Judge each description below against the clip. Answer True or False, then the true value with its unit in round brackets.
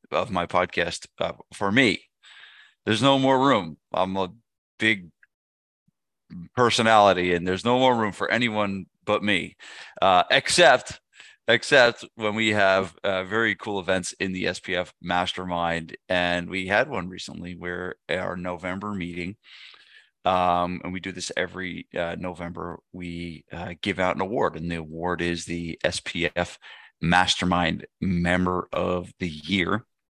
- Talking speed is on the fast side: False (145 wpm)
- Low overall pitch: True (90 Hz)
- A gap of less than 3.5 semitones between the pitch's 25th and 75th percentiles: True (2.9 semitones)